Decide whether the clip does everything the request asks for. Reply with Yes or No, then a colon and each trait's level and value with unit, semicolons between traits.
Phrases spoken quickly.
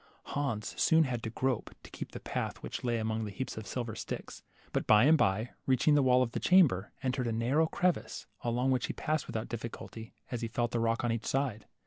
Yes: fast, 235 wpm